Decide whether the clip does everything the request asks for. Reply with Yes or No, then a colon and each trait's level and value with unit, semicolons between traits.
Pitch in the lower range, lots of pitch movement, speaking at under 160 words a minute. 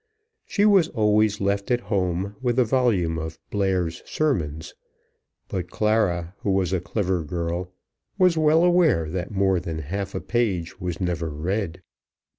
No: very low, 95 Hz; average, 4.6 semitones; average, 150 wpm